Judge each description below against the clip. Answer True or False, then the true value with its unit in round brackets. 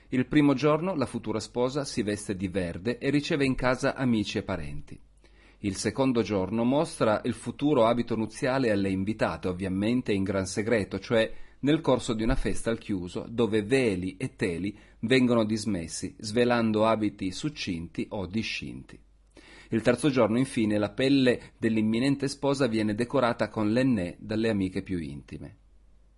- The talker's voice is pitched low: True (110 Hz)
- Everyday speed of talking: True (150 wpm)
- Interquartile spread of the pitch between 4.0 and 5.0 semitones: True (4.3 semitones)